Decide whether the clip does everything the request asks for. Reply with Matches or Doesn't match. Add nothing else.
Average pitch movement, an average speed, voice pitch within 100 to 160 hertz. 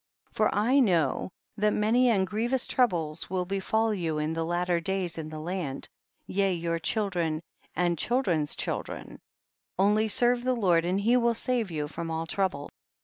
Doesn't match